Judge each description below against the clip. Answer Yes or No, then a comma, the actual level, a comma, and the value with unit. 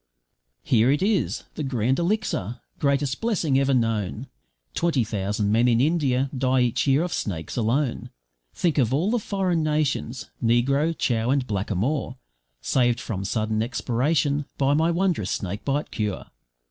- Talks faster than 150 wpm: No, average, 145 wpm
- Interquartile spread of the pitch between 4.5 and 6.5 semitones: Yes, average, 4.9 semitones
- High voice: No, low, 130 Hz